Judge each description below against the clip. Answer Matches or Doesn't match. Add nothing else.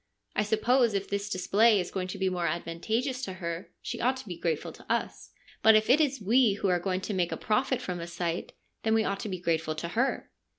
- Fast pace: Matches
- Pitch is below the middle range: Doesn't match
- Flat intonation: Doesn't match